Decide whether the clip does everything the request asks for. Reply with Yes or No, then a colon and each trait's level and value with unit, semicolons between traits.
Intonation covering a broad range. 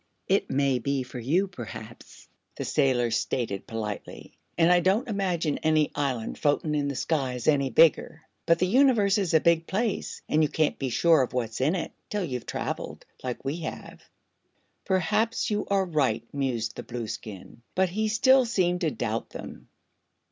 Yes: wide, 6.7 semitones